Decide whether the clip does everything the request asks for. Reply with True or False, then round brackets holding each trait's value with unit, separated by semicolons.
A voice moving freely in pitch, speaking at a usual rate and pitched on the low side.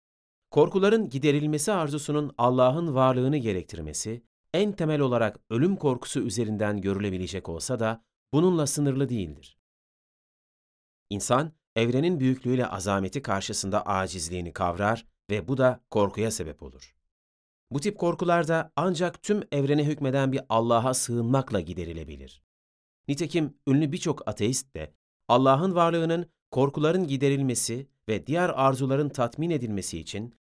True (7.0 semitones; 110 wpm; 125 Hz)